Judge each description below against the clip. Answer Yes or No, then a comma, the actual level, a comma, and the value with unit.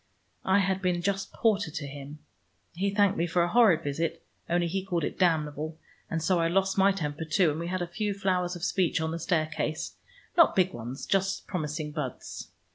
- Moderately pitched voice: Yes, medium, 175 Hz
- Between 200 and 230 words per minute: Yes, fast, 205 wpm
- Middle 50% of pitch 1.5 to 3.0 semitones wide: No, average, 3.4 semitones